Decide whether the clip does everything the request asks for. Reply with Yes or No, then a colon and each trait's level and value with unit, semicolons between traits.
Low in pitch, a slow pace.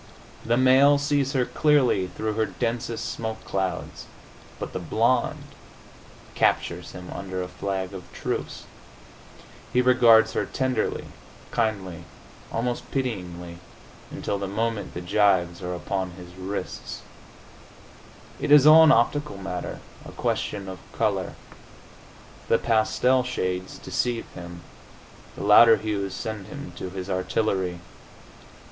Yes: low, 105 Hz; slow, 125 wpm